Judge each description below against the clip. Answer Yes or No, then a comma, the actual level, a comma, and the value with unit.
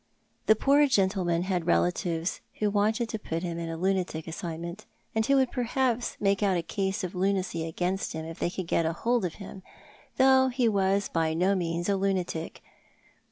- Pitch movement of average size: Yes, average, 4.1 semitones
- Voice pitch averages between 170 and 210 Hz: Yes, high, 190 Hz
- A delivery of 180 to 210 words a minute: Yes, average, 185 wpm